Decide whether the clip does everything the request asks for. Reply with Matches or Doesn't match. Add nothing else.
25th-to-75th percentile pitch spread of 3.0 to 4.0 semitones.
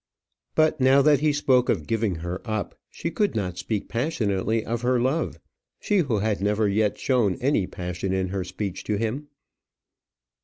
Doesn't match